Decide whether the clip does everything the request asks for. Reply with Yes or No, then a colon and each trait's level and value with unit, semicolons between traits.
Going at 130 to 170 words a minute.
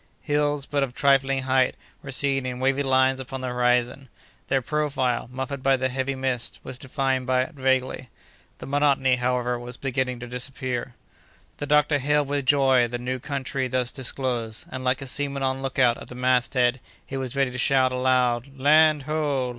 No: average, 180 wpm